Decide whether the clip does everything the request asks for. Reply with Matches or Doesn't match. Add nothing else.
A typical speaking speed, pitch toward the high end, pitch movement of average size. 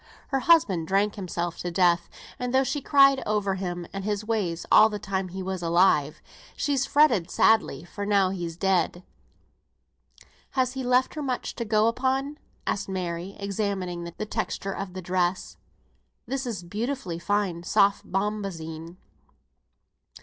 Matches